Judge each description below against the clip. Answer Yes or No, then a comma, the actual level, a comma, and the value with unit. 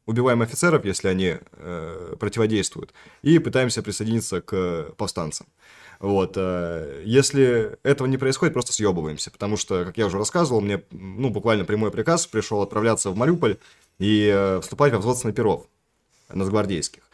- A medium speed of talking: Yes, average, 140 wpm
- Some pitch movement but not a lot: Yes, average, 4.3 semitones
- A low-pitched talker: Yes, low, 110 Hz